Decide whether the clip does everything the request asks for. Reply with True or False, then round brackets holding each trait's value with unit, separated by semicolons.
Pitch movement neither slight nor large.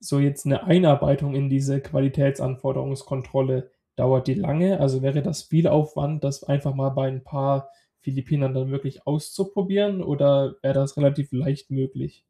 False (1.4 semitones)